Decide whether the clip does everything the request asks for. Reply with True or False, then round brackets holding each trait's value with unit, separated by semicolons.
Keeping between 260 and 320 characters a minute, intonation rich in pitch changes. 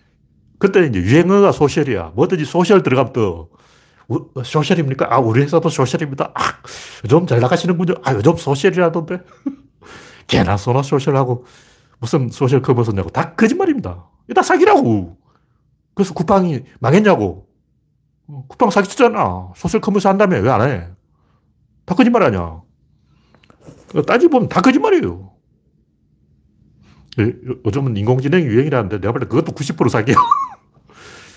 True (300 characters per minute; 7.4 semitones)